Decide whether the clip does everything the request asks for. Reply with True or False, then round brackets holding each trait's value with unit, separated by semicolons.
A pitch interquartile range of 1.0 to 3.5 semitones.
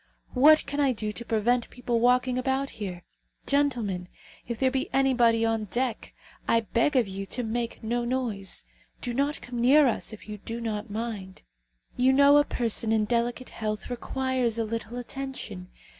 True (3.0 semitones)